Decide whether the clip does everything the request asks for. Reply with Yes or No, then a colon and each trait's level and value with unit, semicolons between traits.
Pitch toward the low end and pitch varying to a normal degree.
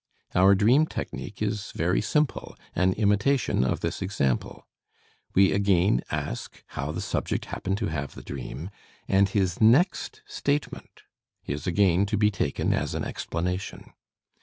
Yes: low, 100 Hz; average, 3.2 semitones